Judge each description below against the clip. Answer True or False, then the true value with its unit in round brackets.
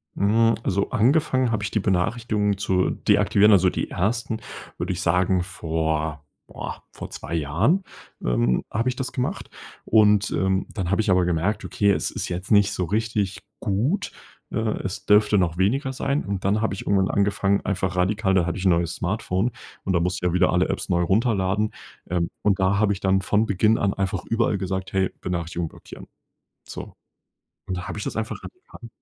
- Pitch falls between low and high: False (95 Hz)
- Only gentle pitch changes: False (3.0 semitones)